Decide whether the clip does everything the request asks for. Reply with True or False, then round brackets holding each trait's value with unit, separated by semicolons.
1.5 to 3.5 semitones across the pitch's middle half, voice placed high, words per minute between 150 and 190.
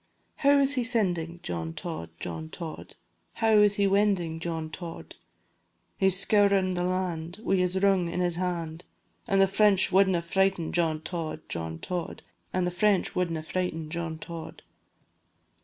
False (3.0 semitones; 180 Hz; 155 wpm)